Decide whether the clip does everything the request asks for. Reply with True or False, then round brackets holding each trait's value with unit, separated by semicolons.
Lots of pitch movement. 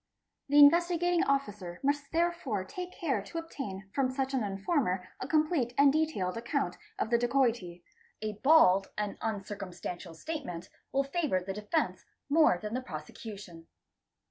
True (7.2 semitones)